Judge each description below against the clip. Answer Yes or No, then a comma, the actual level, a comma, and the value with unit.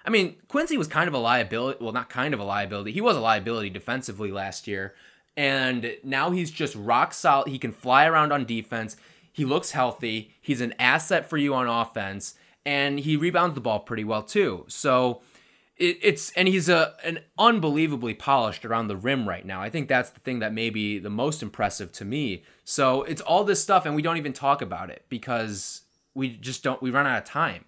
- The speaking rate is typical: No, fast, 215 wpm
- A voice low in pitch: Yes, low, 130 Hz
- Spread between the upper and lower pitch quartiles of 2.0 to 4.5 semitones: No, average, 5.2 semitones